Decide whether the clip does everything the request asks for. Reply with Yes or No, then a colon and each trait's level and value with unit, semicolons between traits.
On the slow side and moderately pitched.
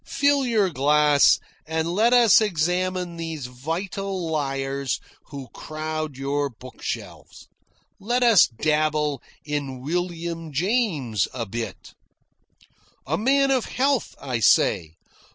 Yes: slow, 110 wpm; medium, 155 Hz